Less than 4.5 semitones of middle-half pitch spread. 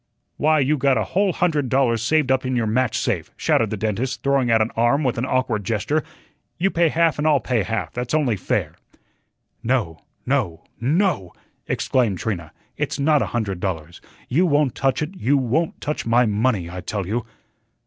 No: average, 4.9 semitones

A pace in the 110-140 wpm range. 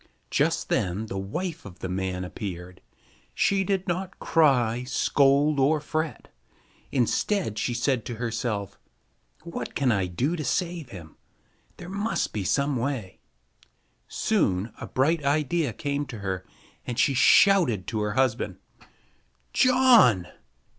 Yes: slow, 135 wpm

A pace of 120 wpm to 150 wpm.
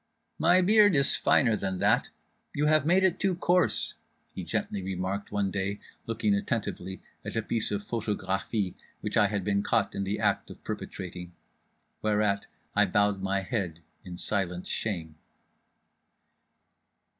Yes: average, 145 wpm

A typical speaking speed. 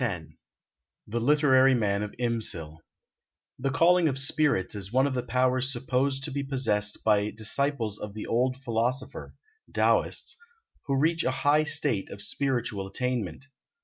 Yes: average, 145 wpm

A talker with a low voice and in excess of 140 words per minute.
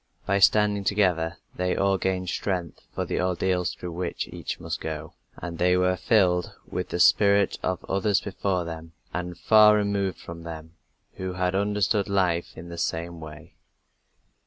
Yes: very low, 90 Hz; average, 160 wpm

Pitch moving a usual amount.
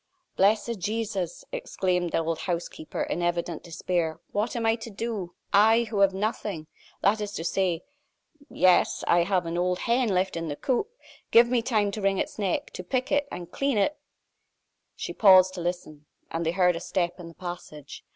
Yes: average, 4.0 semitones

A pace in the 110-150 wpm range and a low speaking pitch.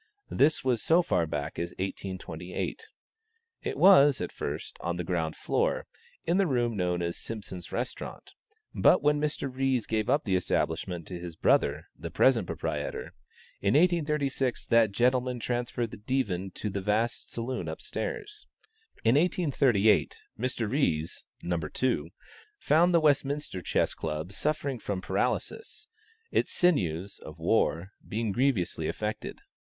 Yes: average, 140 wpm; low, 115 Hz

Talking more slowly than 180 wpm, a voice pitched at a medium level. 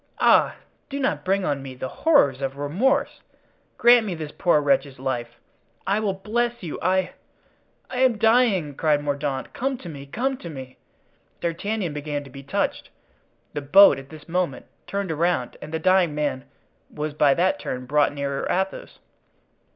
Yes: average, 165 wpm; medium, 155 Hz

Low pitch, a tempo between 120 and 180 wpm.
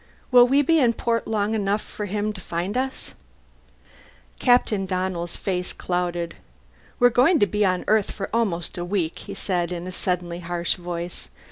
No: high, 195 Hz; average, 170 wpm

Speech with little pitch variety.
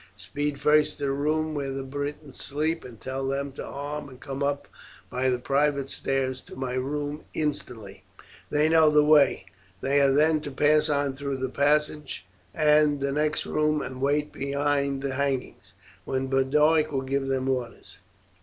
Yes: narrow, 2.0 semitones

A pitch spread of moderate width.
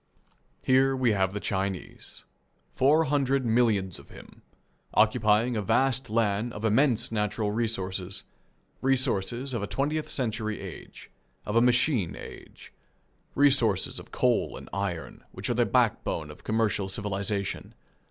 Yes: average, 4.4 semitones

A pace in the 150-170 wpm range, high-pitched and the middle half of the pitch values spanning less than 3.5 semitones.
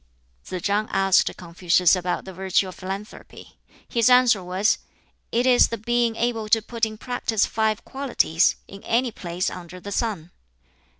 No: average, 160 wpm; high, 210 Hz; average, 4.1 semitones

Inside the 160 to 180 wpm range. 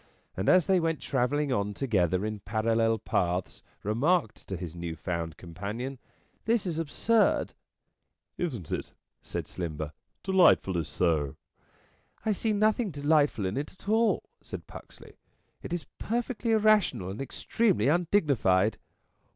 No: average, 145 wpm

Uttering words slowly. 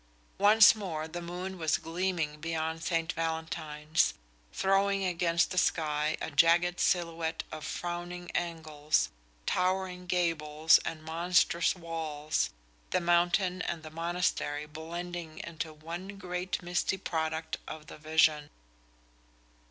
Yes: slow, 115 wpm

